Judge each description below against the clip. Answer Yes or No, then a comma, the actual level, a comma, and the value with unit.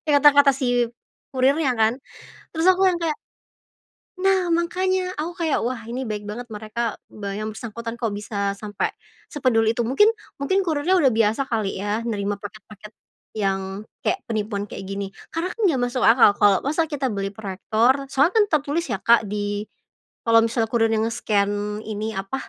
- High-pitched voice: Yes, high, 230 Hz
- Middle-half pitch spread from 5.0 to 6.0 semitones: Yes, average, 5.3 semitones